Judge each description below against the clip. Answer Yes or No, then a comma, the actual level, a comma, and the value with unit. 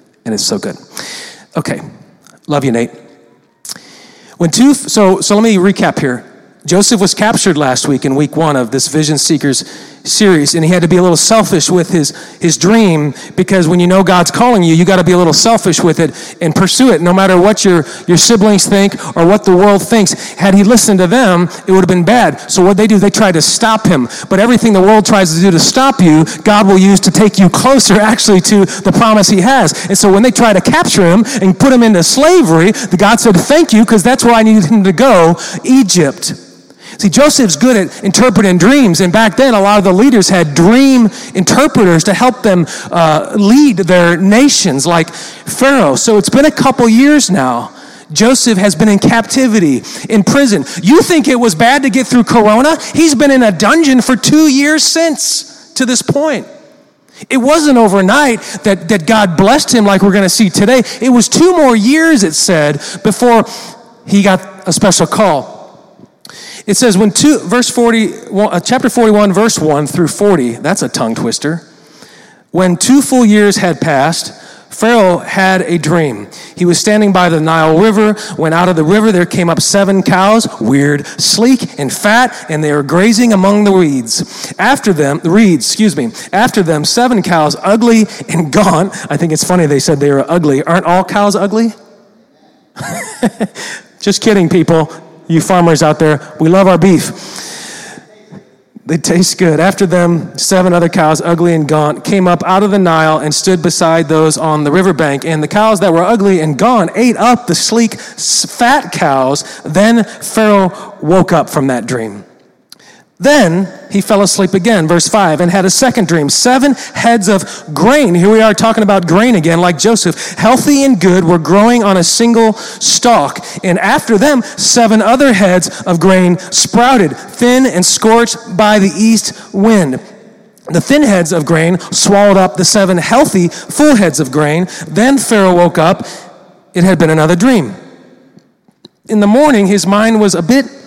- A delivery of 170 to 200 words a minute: Yes, average, 190 wpm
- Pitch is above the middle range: Yes, high, 195 Hz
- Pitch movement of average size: Yes, average, 5.0 semitones